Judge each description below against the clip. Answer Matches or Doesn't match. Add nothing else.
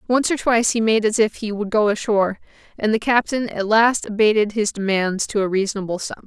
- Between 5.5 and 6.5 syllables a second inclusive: Matches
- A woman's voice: Matches